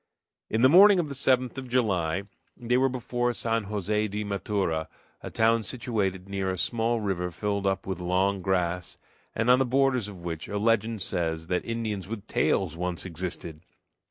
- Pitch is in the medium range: No, low, 105 Hz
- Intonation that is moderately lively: Yes, average, 4.4 semitones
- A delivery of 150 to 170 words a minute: No, average, 180 wpm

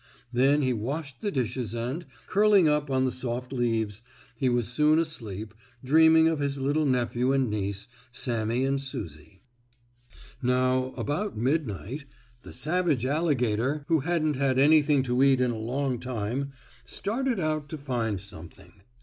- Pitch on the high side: No, low, 130 Hz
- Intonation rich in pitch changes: No, average, 4.0 semitones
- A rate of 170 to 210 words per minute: No, average, 150 wpm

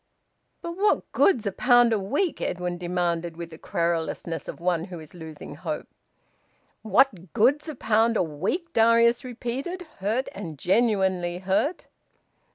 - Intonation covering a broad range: Yes, wide, 5.8 semitones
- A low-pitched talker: No, high, 200 Hz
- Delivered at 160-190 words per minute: No, average, 145 wpm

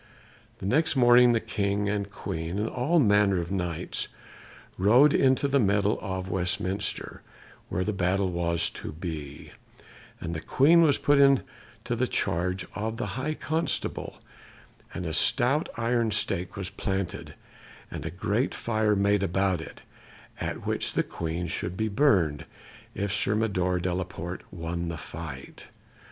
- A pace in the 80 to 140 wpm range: No, average, 150 wpm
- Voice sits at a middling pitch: No, low, 100 Hz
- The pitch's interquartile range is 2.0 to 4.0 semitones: No, average, 4.8 semitones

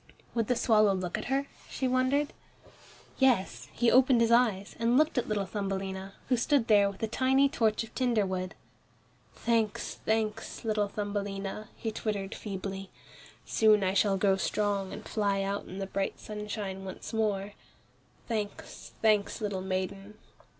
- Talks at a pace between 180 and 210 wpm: No, average, 155 wpm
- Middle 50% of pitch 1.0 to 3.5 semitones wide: Yes, average, 2.8 semitones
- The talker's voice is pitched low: No, high, 210 Hz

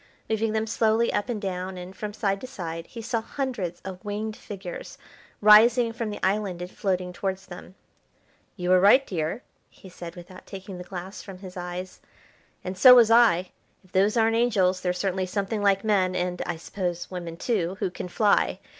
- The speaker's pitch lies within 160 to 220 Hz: Yes, high, 190 Hz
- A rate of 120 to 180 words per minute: No, average, 190 wpm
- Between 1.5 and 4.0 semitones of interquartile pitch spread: Yes, average, 3.2 semitones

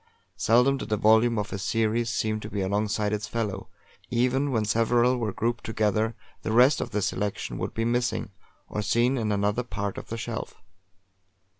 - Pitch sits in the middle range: No, low, 110 Hz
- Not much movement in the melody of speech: Yes, narrow, 2.2 semitones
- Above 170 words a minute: Yes, average, 180 wpm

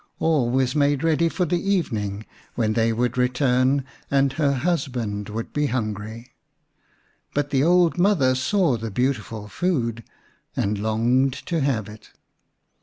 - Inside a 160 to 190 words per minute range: No, average, 145 wpm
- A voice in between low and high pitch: No, low, 130 Hz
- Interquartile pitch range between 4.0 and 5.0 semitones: Yes, average, 4.7 semitones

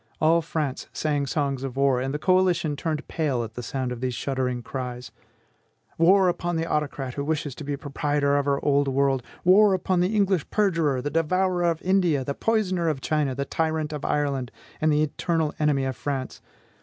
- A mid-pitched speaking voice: Yes, medium, 150 Hz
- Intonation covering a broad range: No, average, 3.6 semitones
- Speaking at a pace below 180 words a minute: No, average, 195 wpm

